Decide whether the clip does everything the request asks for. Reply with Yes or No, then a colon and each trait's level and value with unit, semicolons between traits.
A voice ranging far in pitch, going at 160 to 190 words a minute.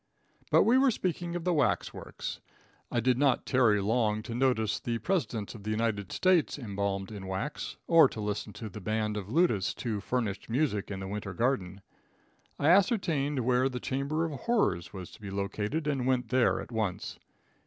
Yes: wide, 5.7 semitones; average, 180 wpm